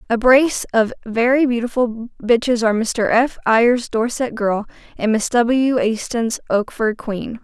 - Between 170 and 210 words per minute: No, average, 145 wpm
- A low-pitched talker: No, high, 235 Hz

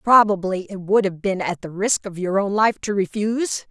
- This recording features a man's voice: No, female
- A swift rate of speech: Yes, fast, 225 wpm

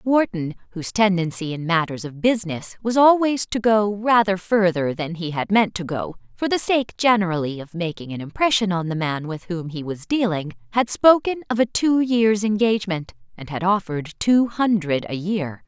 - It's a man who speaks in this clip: No, female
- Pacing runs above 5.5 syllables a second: No, 5.0 syllables/s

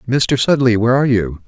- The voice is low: Yes, low, 120 Hz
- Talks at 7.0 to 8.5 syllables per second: No, 6.4 syllables/s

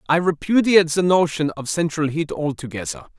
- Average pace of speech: Yes, average, 150 wpm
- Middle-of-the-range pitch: Yes, medium, 155 Hz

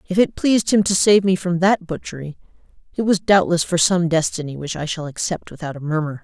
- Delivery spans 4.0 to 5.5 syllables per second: No, 5.8 syllables/s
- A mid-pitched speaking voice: Yes, medium, 175 Hz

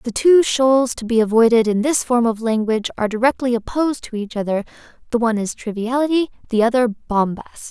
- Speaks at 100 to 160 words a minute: No, average, 185 wpm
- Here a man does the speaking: No, female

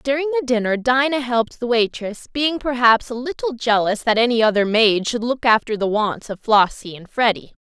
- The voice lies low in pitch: No, high, 240 Hz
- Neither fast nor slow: Yes, average, 195 wpm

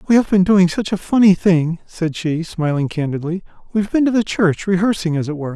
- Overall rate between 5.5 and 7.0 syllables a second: Yes, 5.7 syllables/s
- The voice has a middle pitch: Yes, medium, 180 Hz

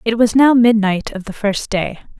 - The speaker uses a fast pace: Yes, fast, 220 wpm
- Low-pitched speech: No, high, 220 Hz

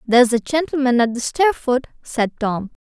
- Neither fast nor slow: Yes, average, 170 wpm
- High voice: Yes, very high, 250 Hz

